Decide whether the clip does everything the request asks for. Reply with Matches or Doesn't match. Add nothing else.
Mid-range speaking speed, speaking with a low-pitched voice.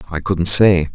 Matches